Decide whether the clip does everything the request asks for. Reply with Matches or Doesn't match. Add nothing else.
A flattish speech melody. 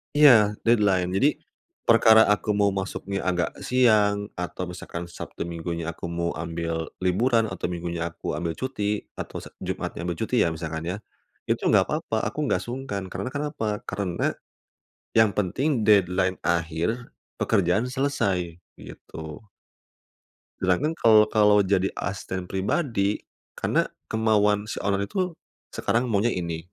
Doesn't match